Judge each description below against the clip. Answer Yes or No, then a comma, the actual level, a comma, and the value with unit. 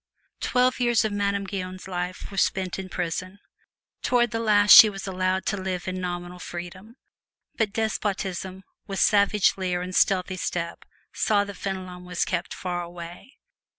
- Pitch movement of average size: No, narrow, 2.2 semitones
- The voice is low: No, high, 190 Hz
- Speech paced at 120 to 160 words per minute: Yes, average, 155 wpm